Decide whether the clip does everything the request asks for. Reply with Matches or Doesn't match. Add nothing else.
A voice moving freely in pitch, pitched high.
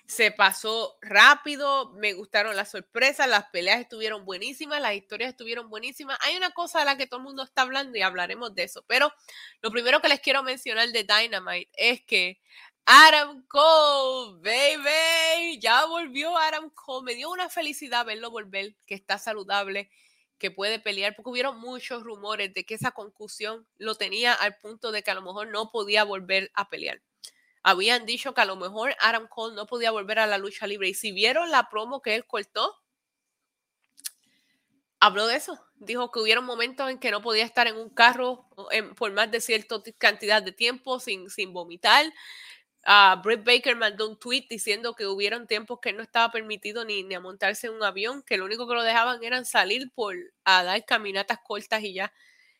Doesn't match